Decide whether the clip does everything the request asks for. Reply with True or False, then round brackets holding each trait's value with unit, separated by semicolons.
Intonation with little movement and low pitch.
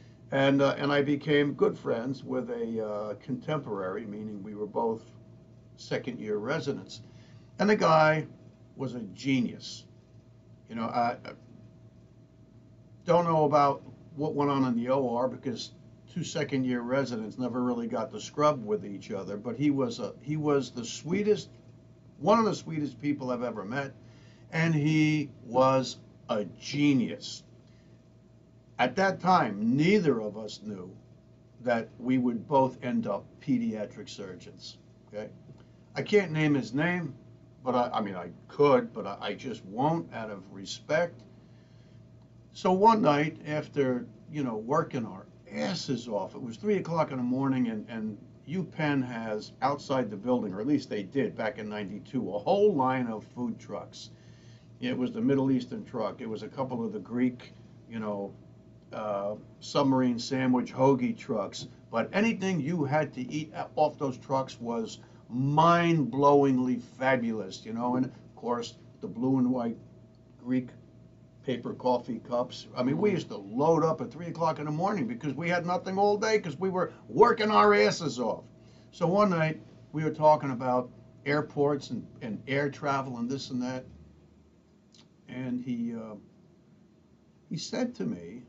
False (4.3 semitones; 130 Hz)